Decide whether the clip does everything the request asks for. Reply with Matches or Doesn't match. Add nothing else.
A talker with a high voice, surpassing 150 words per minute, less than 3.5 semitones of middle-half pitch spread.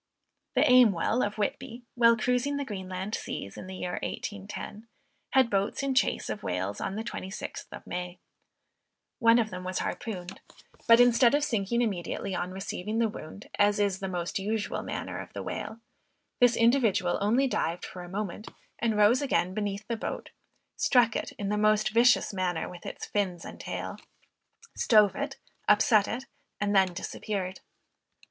Doesn't match